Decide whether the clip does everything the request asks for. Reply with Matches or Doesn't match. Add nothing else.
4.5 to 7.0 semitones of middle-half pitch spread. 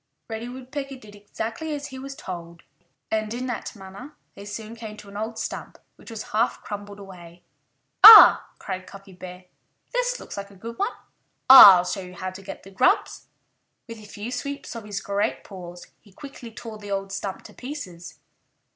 Doesn't match